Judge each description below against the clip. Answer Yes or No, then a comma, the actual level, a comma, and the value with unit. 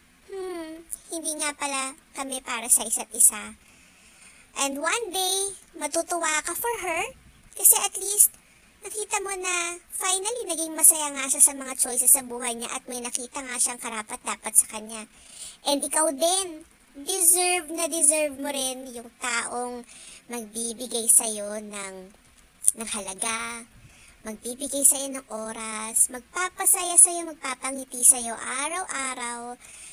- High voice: Yes, very high, 270 Hz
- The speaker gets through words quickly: No, average, 130 wpm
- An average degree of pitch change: No, wide, 6.0 semitones